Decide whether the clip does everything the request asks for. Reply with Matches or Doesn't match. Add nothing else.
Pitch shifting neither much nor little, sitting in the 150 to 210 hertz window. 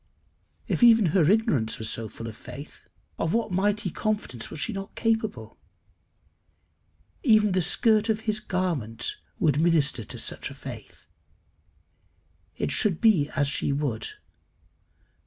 Doesn't match